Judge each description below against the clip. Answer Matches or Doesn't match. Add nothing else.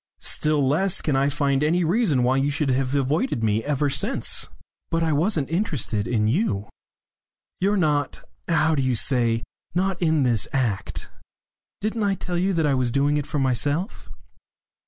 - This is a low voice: Doesn't match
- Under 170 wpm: Doesn't match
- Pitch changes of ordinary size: Matches